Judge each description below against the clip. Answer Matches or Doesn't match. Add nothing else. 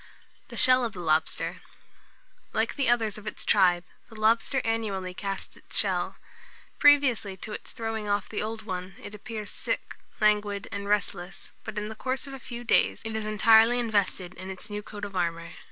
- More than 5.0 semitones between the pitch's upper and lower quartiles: Doesn't match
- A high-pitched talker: Matches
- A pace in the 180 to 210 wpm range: Matches